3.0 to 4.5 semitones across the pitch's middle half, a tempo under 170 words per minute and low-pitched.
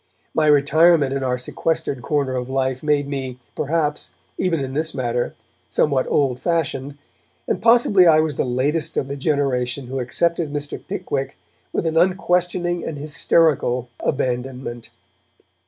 No: average, 3.6 semitones; average, 140 wpm; medium, 145 Hz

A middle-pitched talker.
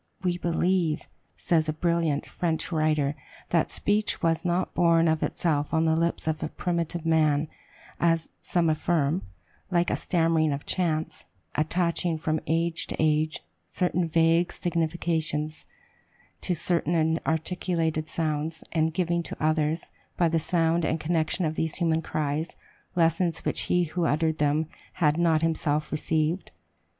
Yes: medium, 160 Hz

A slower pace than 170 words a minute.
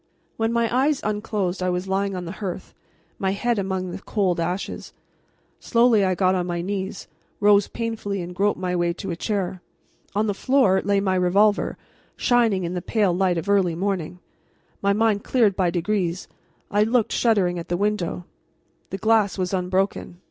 No: average, 175 wpm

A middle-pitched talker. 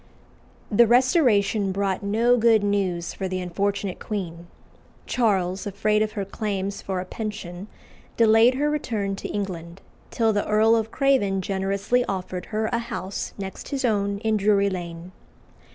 No: high, 200 Hz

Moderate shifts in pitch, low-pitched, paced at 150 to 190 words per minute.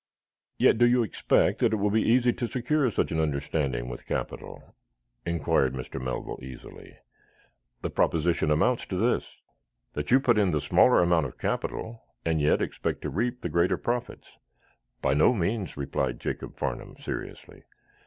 No: wide, 8.2 semitones; very low, 85 Hz; average, 165 wpm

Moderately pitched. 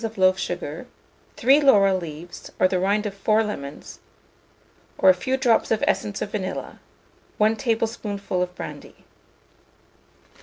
No: high, 200 Hz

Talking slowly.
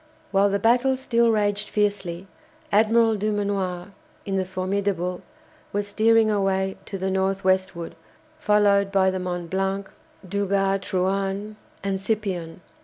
Yes: slow, 125 wpm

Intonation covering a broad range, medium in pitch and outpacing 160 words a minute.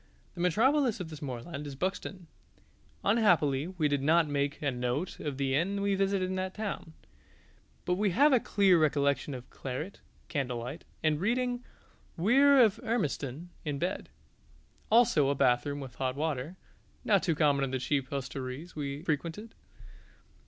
No: wide, 5.9 semitones; medium, 155 Hz; average, 155 wpm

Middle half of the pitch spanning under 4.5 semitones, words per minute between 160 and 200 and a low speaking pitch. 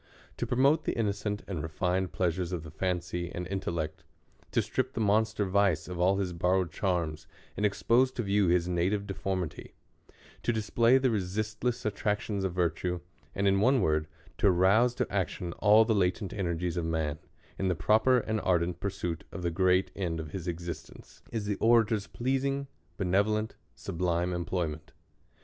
Yes: average, 3.7 semitones; average, 170 wpm; very low, 95 Hz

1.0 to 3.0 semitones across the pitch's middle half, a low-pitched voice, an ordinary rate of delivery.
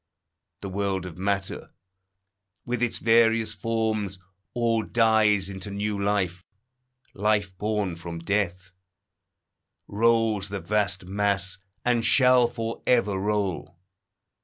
No: average, 2.7 semitones; low, 105 Hz; slow, 110 wpm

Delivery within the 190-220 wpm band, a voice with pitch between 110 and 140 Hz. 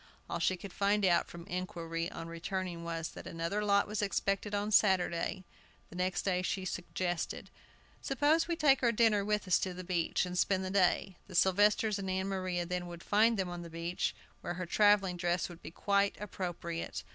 No: average, 195 wpm; medium, 185 Hz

